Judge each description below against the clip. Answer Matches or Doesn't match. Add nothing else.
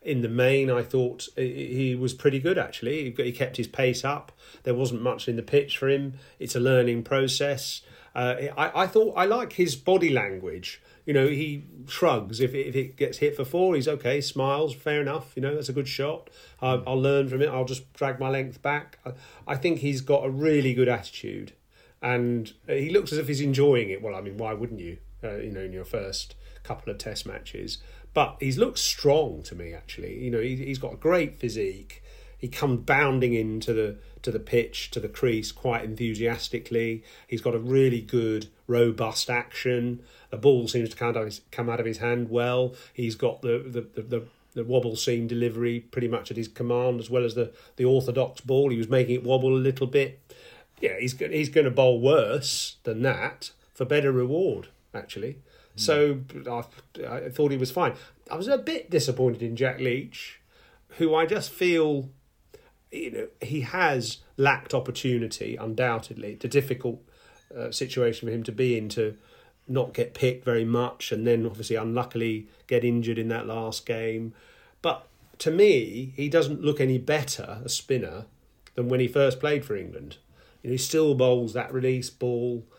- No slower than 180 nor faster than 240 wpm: Matches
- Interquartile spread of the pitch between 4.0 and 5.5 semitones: Doesn't match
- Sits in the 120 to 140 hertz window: Matches